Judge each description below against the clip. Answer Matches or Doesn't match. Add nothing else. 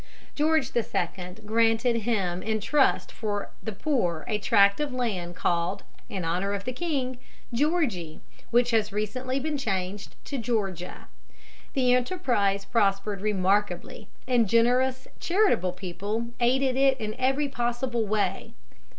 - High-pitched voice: Matches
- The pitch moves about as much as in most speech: Matches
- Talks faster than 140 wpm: Doesn't match